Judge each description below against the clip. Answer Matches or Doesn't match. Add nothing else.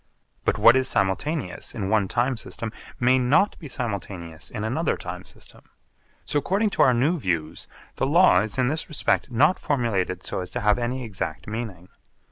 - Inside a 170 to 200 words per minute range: Matches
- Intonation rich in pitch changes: Matches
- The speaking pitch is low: Matches